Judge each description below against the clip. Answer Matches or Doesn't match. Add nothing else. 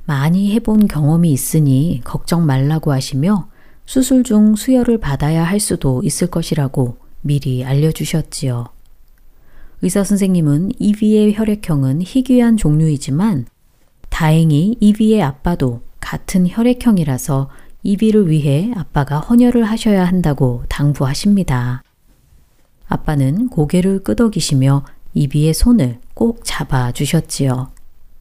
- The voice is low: Doesn't match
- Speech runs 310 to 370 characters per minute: Doesn't match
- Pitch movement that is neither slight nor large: Doesn't match